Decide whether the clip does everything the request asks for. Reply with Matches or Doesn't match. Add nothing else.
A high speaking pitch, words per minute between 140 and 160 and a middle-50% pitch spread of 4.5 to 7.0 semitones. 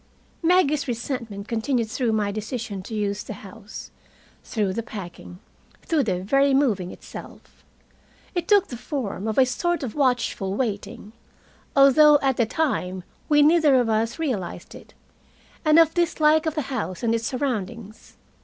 Matches